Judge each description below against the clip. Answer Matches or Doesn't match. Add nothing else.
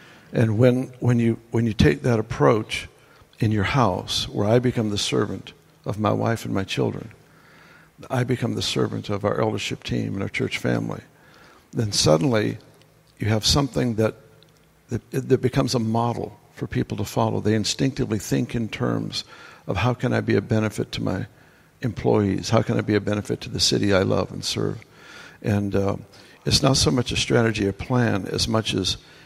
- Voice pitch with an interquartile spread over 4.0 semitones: Doesn't match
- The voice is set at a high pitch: Doesn't match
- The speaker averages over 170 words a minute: Matches